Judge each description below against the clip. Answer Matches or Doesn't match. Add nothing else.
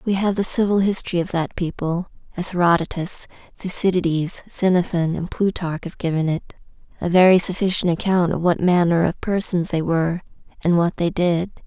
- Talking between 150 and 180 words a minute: Matches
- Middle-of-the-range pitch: Matches